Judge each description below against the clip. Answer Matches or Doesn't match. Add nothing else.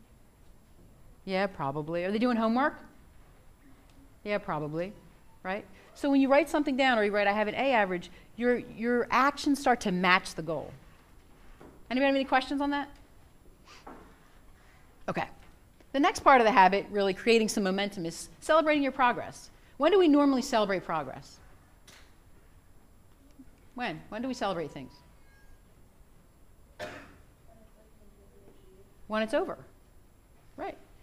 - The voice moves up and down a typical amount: Doesn't match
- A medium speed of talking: Doesn't match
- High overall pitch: Matches